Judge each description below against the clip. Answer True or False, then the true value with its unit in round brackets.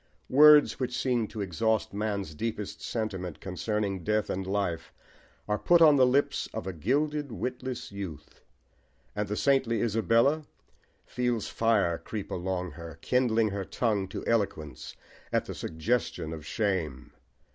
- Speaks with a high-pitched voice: False (105 Hz)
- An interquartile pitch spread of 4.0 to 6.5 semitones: True (4.8 semitones)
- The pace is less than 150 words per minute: True (140 wpm)